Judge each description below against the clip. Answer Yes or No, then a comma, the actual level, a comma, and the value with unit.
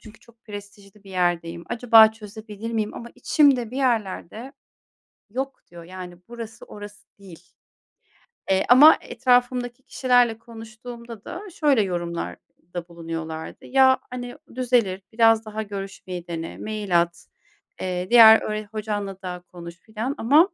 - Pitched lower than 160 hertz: No, high, 215 Hz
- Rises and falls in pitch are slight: No, average, 4.6 semitones